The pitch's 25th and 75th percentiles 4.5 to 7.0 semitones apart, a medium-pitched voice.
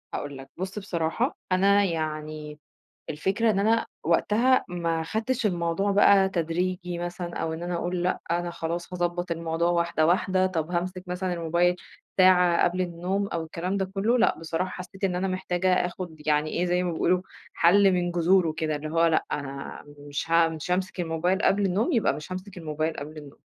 No: narrow, 2.4 semitones; medium, 175 Hz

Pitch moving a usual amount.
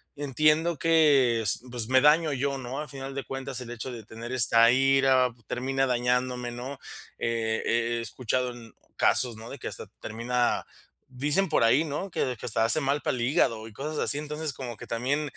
Yes: average, 3.0 semitones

